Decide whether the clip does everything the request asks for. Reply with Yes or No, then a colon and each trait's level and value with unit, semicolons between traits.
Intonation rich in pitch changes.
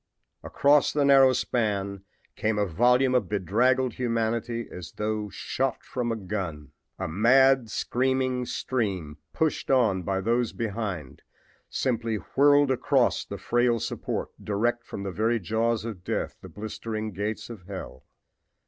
No: average, 3.9 semitones